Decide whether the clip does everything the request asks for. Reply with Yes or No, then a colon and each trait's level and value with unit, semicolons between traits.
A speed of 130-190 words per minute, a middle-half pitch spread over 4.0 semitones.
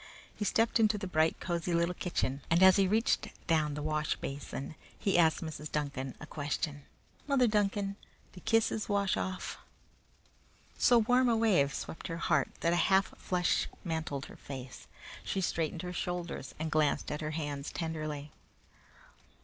Yes: average, 160 wpm; average, 4.6 semitones